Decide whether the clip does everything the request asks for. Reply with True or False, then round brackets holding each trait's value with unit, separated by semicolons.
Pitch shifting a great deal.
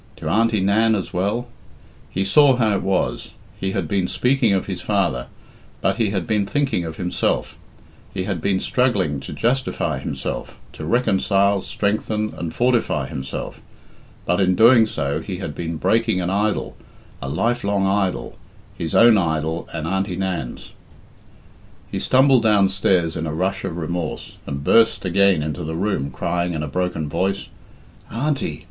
False (4.1 semitones)